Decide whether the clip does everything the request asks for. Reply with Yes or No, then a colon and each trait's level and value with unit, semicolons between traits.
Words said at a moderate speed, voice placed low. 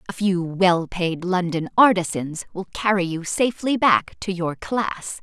No: average, 160 wpm; medium, 185 Hz